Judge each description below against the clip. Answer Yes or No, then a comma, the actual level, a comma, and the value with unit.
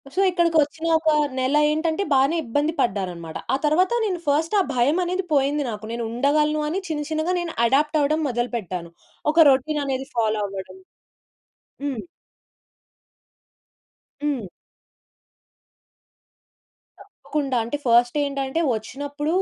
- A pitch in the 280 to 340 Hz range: Yes, very high, 285 Hz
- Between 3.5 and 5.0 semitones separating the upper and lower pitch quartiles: Yes, average, 4.7 semitones